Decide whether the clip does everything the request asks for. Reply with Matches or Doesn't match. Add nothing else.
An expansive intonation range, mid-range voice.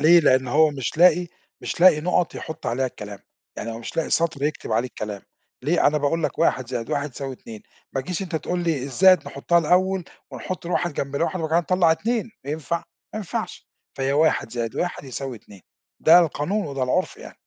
Doesn't match